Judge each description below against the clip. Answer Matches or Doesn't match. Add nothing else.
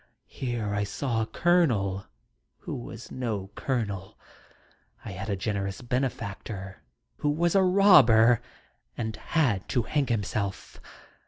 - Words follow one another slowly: Matches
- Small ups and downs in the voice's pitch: Doesn't match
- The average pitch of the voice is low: Matches